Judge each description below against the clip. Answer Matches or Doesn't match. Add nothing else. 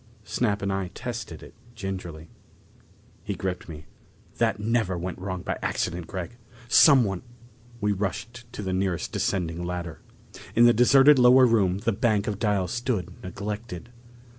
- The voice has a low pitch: Matches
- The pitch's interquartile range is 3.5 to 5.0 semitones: Matches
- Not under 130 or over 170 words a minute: Matches